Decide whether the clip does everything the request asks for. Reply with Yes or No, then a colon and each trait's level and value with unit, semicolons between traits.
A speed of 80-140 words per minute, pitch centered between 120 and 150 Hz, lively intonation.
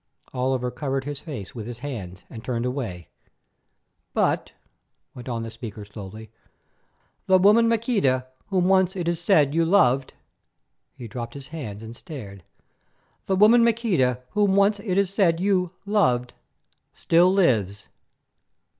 Yes: slow, 135 wpm; medium, 140 Hz; wide, 8.2 semitones